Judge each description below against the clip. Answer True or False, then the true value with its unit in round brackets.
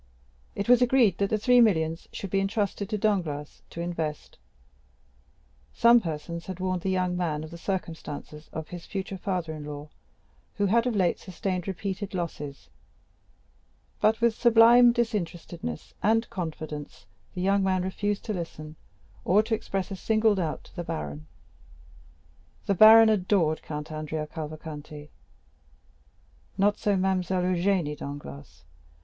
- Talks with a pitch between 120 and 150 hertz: False (185 Hz)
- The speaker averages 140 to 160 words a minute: True (145 wpm)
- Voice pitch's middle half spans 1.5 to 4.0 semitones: False (4.6 semitones)